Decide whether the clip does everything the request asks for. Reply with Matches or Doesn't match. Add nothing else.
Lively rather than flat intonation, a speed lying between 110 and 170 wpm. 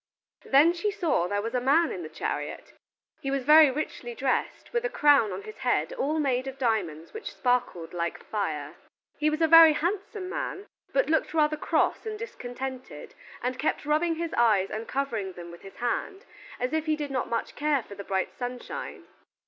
Doesn't match